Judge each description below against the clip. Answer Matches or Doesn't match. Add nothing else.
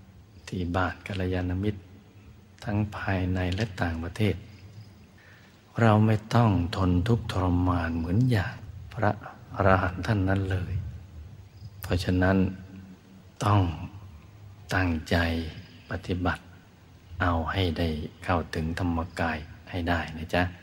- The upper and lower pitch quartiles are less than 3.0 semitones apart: Matches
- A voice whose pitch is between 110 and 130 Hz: Doesn't match